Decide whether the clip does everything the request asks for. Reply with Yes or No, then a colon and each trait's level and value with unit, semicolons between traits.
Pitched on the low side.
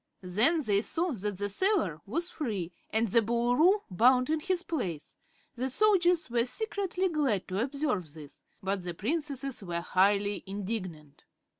No: high, 235 Hz